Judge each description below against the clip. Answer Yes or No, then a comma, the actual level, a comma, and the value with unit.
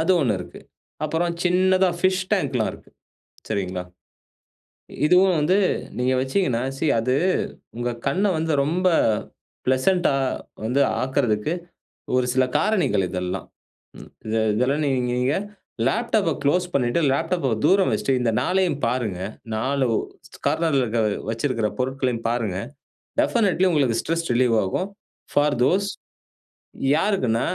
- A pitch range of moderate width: No, wide, 6.8 semitones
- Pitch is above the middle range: No, low, 135 Hz